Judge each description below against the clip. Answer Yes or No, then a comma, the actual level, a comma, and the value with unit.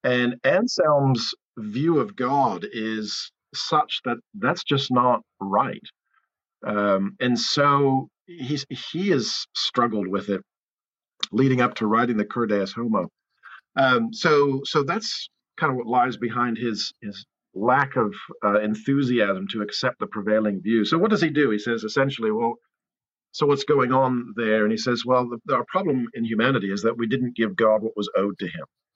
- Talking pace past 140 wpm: Yes, average, 170 wpm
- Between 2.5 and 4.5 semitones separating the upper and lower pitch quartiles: Yes, average, 4.2 semitones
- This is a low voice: Yes, low, 120 Hz